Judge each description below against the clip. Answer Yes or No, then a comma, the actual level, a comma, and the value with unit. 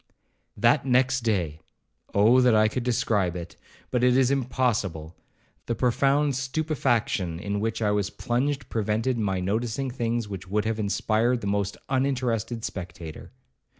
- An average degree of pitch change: Yes, average, 3.8 semitones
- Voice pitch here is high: No, low, 115 Hz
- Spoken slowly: Yes, slow, 130 wpm